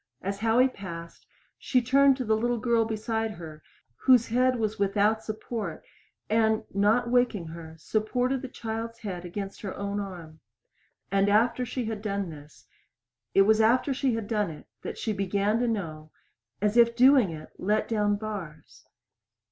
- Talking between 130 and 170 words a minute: Yes, average, 165 wpm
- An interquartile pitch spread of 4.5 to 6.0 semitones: No, average, 3.1 semitones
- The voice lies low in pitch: No, high, 215 Hz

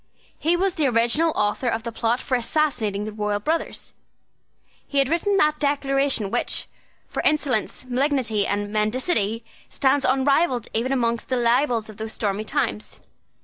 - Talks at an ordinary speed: Yes, average, 150 wpm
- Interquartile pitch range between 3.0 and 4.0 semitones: No, average, 4.7 semitones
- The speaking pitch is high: Yes, very high, 250 Hz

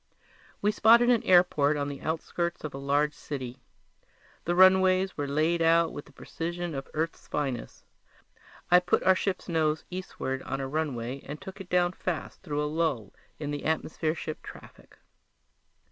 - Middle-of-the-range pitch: Yes, medium, 160 Hz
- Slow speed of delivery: No, average, 165 wpm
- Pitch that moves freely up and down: No, average, 3.7 semitones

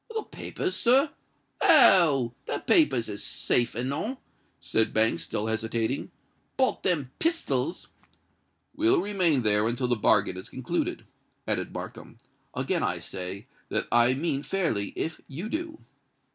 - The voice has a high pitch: No, low, 135 Hz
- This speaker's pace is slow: Yes, slow, 130 wpm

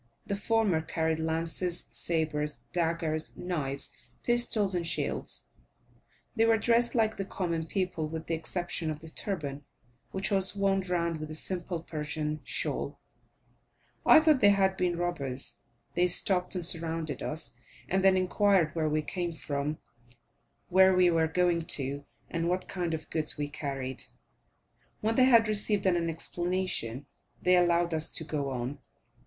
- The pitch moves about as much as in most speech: Yes, average, 3.3 semitones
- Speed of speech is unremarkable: Yes, average, 150 wpm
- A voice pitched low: No, medium, 170 Hz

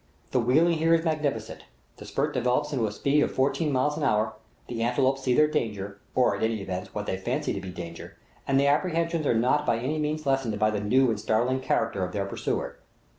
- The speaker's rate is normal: No, fast, 225 wpm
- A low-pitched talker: Yes, low, 125 Hz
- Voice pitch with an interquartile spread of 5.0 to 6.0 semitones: Yes, wide, 5.5 semitones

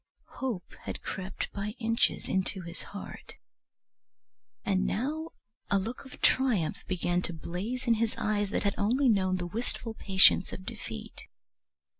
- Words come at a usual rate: Yes, average, 145 wpm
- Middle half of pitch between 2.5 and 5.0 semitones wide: Yes, average, 3.7 semitones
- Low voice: No, high, 205 Hz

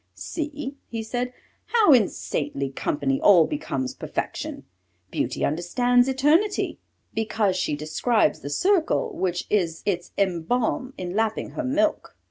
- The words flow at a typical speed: No, slow, 125 wpm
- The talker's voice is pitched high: Yes, high, 220 Hz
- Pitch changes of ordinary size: No, wide, 8.0 semitones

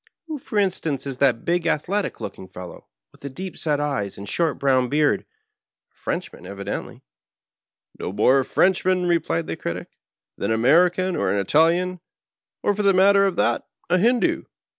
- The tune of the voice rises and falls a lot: Yes, wide, 6.2 semitones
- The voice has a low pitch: No, medium, 165 Hz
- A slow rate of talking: No, average, 185 wpm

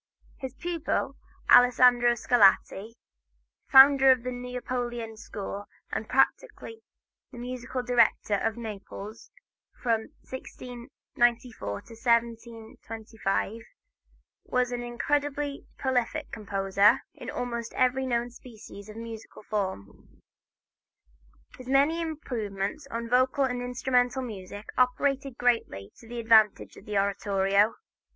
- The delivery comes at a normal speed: No, slow, 105 wpm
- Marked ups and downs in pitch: No, average, 2.8 semitones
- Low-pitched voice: No, high, 240 Hz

